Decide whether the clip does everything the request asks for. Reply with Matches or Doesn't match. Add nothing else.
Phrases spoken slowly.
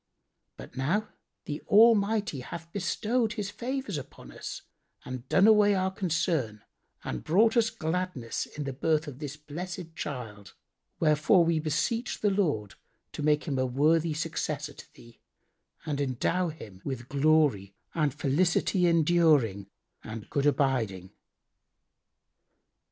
Matches